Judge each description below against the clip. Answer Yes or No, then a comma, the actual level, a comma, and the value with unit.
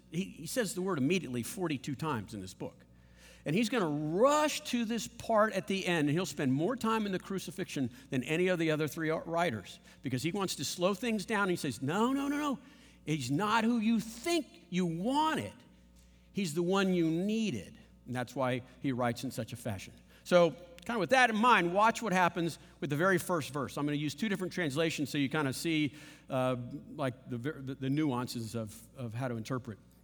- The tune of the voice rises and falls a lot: Yes, wide, 7.0 semitones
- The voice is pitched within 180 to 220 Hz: No, medium, 160 Hz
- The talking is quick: Yes, fast, 220 wpm